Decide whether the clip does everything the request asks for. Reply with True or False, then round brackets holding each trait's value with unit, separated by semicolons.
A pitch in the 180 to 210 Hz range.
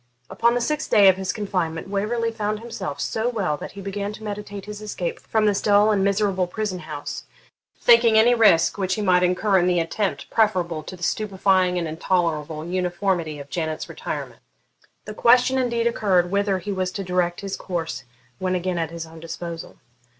True (190 Hz)